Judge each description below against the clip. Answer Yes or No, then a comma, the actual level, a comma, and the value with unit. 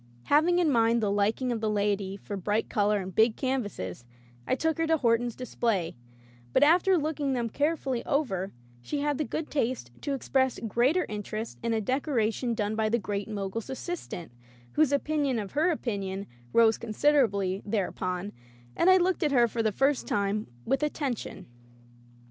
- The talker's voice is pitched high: Yes, high, 235 Hz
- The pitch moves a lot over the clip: Yes, wide, 5.7 semitones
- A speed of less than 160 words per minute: No, average, 175 wpm